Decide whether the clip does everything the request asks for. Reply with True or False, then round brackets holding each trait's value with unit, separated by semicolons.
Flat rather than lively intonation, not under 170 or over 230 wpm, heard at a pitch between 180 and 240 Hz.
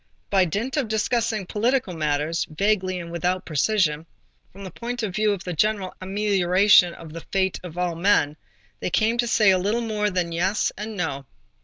False (3.8 semitones; 185 wpm; 190 Hz)